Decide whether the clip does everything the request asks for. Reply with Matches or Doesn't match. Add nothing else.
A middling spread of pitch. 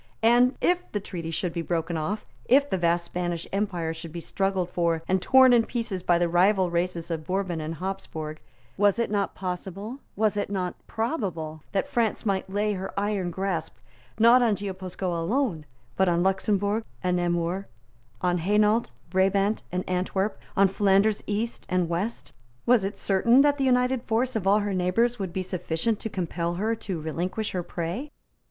Matches